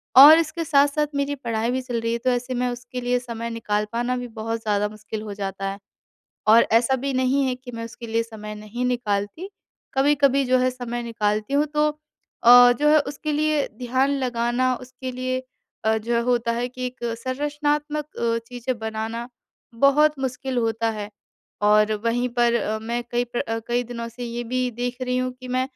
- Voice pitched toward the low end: No, high, 245 Hz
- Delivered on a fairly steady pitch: Yes, narrow, 2.1 semitones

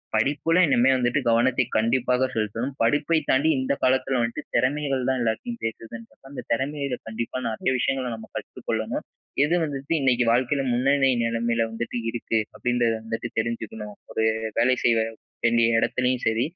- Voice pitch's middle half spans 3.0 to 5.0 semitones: No, narrow, 2.6 semitones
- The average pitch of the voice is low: Yes, low, 125 Hz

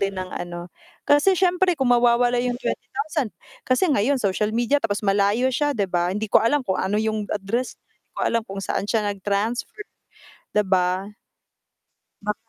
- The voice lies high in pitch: Yes, high, 220 Hz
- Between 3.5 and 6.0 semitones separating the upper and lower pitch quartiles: Yes, average, 4.5 semitones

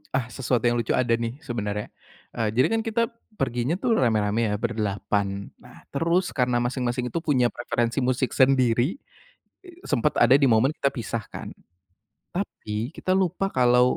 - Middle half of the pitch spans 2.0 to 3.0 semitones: Yes, narrow, 2.5 semitones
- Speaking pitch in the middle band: No, low, 120 Hz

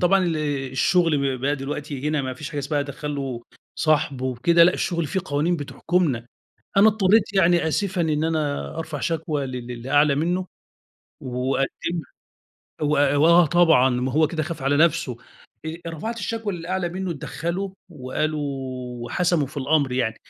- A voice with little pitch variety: No, average, 3.9 semitones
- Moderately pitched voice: Yes, medium, 155 Hz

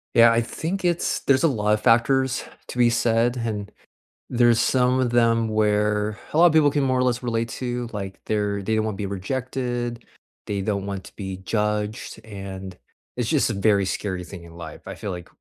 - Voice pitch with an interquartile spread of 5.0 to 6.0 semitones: No, average, 3.3 semitones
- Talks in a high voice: No, low, 115 Hz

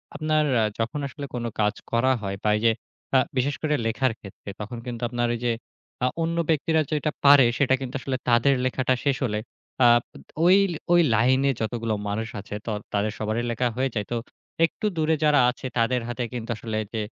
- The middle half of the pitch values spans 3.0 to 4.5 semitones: Yes, average, 3.9 semitones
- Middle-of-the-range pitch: No, low, 125 Hz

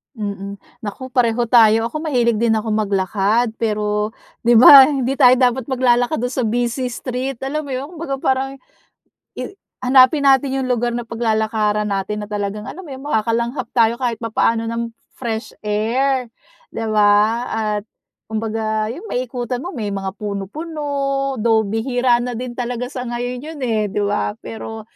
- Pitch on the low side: No, high, 235 Hz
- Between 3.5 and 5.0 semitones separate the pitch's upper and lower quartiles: No, average, 3.0 semitones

